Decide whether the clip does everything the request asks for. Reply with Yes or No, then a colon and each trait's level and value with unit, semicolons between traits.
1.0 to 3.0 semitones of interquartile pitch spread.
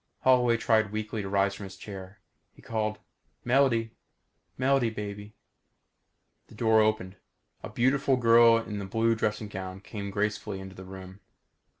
Yes: average, 2.7 semitones